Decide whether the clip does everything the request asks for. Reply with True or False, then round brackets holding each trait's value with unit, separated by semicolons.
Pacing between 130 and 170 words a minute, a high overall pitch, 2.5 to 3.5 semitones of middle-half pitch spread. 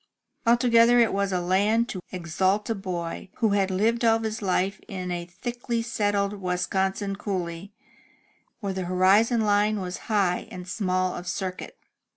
True (155 wpm; 195 Hz; 3.1 semitones)